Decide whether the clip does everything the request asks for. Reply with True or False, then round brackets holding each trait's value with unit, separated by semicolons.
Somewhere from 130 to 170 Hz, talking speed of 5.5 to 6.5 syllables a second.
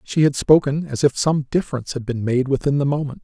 True (140 Hz; 6.1 syllables/s)